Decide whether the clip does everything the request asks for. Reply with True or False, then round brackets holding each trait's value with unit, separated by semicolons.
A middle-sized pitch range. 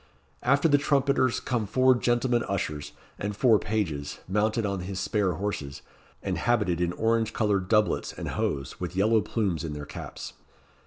True (4.7 semitones)